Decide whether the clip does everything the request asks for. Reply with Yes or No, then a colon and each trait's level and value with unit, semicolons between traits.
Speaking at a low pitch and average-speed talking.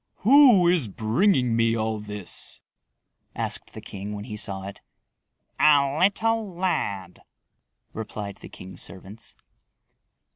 No: low, 115 Hz; slow, 115 wpm